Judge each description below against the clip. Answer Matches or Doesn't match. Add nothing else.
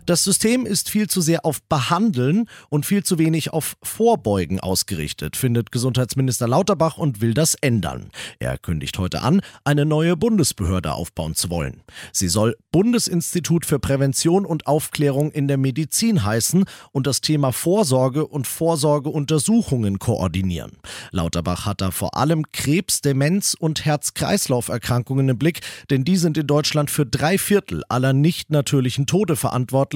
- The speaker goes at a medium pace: Matches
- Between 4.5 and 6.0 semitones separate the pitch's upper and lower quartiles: Matches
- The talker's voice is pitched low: Doesn't match